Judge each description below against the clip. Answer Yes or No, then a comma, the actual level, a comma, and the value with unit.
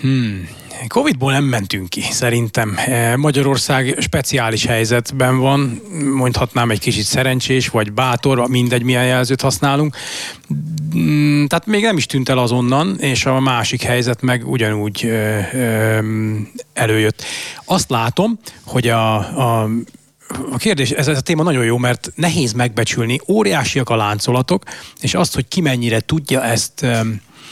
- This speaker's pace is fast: No, slow, 135 wpm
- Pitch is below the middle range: Yes, low, 125 Hz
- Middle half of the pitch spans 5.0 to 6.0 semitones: No, average, 3.2 semitones